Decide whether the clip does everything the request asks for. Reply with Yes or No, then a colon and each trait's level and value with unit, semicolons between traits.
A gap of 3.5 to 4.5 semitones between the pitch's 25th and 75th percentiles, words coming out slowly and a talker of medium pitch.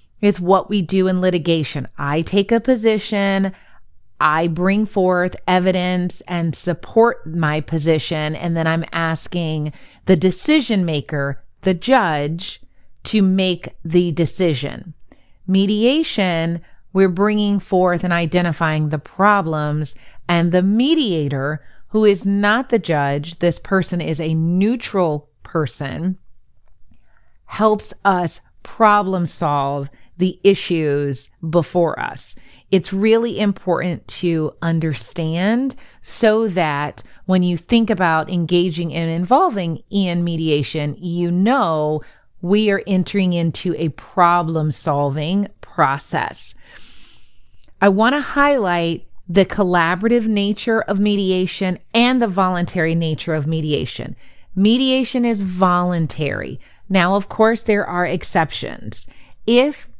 Yes: average, 3.9 semitones; slow, 110 wpm; medium, 180 Hz